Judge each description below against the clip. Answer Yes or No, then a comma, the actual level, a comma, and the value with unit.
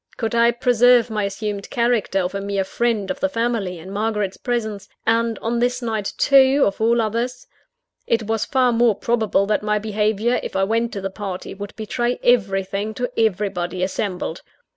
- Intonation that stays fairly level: No, average, 3.1 semitones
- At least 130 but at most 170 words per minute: No, average, 180 wpm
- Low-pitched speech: No, high, 220 Hz